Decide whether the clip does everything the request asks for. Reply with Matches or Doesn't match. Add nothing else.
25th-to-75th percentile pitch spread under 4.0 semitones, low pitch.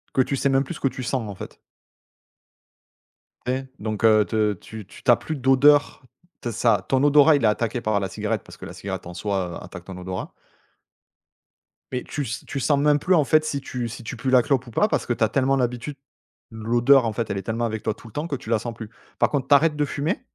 Doesn't match